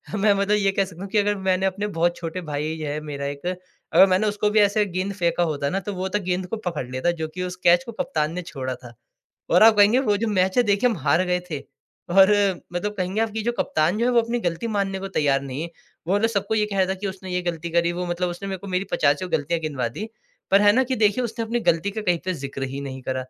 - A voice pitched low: No, medium, 185 Hz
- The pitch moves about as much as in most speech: Yes, average, 4.0 semitones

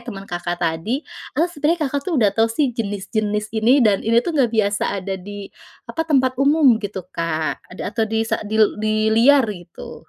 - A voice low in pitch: No, high, 220 Hz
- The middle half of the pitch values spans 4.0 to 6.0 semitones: Yes, average, 4.5 semitones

